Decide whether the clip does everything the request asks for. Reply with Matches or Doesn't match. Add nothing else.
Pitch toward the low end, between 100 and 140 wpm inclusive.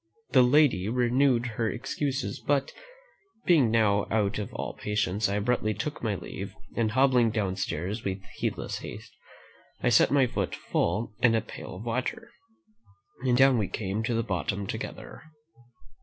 Doesn't match